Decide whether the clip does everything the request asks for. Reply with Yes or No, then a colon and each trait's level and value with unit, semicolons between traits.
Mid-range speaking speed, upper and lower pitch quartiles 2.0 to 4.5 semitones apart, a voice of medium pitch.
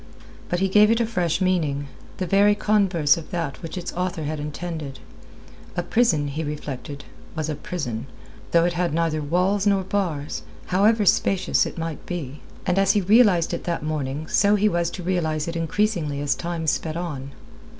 Yes: average, 180 wpm; average, 4.1 semitones; medium, 170 Hz